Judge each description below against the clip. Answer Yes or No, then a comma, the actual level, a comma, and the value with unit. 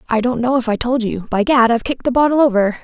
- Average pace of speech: No, fast, 275 wpm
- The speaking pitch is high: Yes, high, 240 Hz